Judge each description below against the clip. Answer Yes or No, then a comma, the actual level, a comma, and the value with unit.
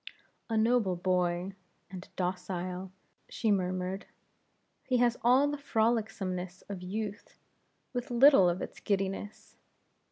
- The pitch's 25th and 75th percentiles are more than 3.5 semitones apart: Yes, average, 4.0 semitones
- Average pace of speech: No, slow, 115 wpm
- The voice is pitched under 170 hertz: No, high, 195 Hz